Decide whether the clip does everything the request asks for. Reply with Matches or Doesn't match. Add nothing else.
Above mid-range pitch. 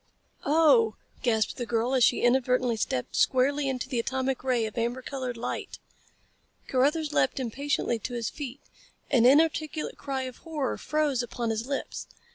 Matches